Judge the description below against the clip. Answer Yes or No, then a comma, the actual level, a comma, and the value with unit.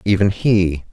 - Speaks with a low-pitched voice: Yes, very low, 95 Hz